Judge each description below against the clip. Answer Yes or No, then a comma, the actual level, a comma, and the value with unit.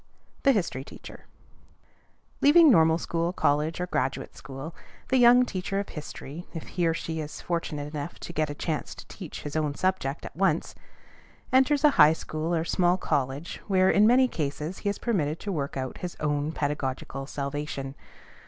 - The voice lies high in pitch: No, medium, 160 Hz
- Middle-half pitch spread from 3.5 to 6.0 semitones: Yes, average, 4.4 semitones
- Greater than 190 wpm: No, average, 175 wpm